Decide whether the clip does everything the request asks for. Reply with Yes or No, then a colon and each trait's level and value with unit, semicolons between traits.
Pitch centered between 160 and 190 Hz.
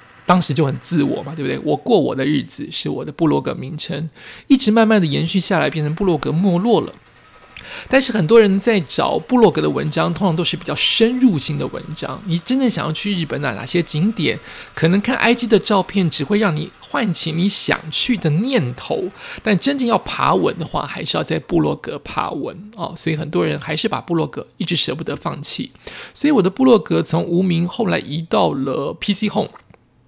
Yes: medium, 185 Hz